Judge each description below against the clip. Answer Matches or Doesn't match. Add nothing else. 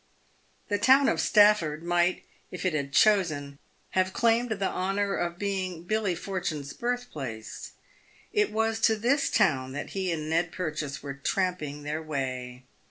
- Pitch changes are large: Matches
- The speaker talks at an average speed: Matches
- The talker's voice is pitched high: Doesn't match